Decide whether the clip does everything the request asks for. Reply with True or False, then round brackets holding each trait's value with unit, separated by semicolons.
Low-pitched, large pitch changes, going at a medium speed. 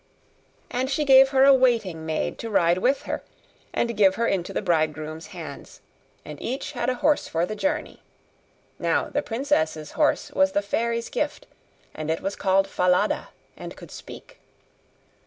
False (215 Hz; 7.2 semitones; 165 wpm)